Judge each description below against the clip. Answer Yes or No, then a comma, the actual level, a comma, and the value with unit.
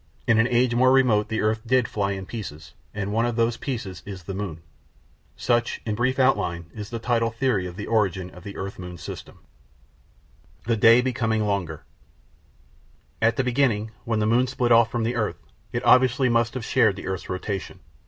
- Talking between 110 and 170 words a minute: No, average, 195 wpm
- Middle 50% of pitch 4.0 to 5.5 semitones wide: No, average, 3.3 semitones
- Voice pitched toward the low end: Yes, low, 110 Hz